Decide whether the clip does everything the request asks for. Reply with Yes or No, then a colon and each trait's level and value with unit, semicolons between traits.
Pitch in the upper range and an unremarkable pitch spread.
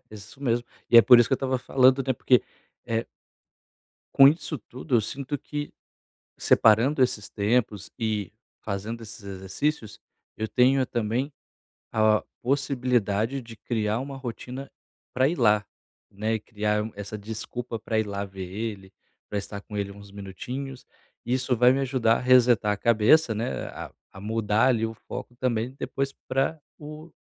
No: low, 115 Hz; average, 3.6 semitones